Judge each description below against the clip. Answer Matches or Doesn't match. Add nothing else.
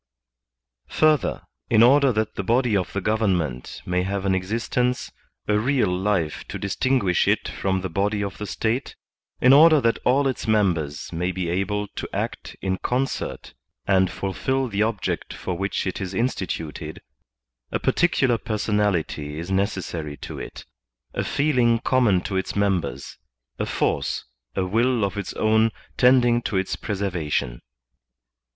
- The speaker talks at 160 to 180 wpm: Doesn't match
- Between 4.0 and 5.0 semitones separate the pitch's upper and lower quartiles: Matches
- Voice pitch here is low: Matches